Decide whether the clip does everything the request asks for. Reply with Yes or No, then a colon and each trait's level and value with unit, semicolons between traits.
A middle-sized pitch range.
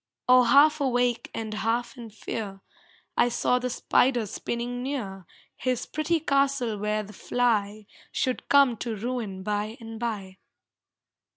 Yes: average, 3.0 semitones